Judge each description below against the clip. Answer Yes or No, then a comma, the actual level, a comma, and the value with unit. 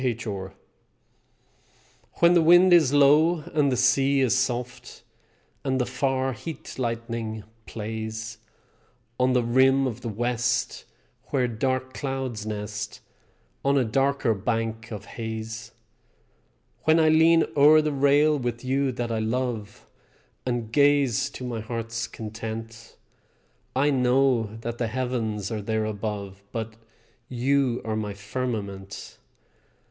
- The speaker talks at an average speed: No, slow, 130 wpm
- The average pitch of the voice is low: Yes, low, 120 Hz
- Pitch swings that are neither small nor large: Yes, average, 3.4 semitones